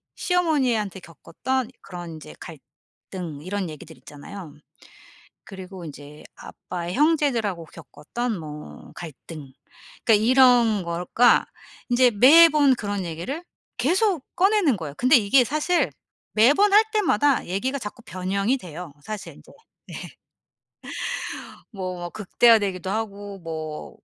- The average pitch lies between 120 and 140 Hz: No, high, 205 Hz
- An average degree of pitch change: No, wide, 7.1 semitones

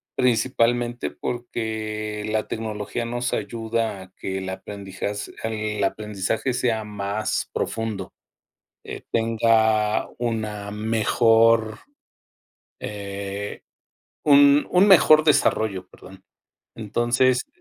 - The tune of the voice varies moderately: No, narrow, 2.3 semitones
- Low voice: Yes, low, 110 Hz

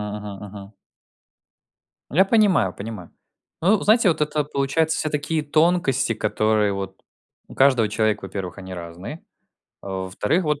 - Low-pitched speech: Yes, low, 115 Hz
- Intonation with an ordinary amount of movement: No, wide, 7.7 semitones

